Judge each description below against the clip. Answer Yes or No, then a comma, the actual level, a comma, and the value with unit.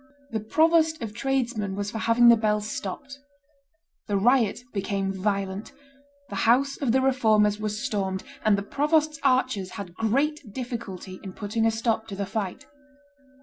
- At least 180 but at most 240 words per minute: No, average, 155 wpm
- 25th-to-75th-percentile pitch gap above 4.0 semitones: Yes, average, 4.4 semitones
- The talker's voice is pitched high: Yes, high, 220 Hz